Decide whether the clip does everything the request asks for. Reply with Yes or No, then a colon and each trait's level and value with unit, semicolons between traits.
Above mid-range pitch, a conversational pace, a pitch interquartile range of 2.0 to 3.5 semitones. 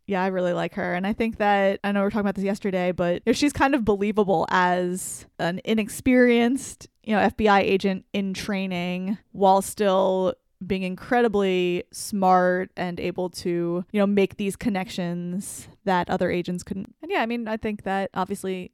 Yes: high, 195 Hz; average, 180 wpm; narrow, 2.5 semitones